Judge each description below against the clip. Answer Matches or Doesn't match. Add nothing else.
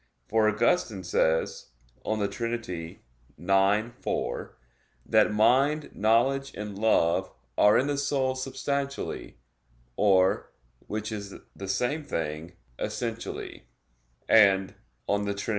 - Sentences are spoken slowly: Matches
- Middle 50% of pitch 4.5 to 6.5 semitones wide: Matches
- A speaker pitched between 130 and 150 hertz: Doesn't match